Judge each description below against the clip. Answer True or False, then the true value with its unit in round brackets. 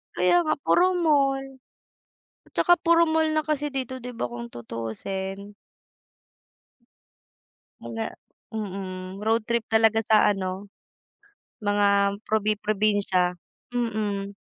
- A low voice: False (210 Hz)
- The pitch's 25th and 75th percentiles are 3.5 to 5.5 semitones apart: True (4.4 semitones)